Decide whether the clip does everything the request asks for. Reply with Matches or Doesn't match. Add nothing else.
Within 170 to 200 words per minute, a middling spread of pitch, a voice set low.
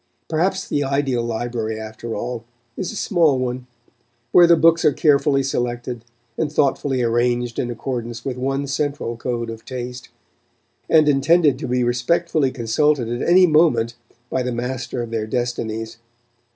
Doesn't match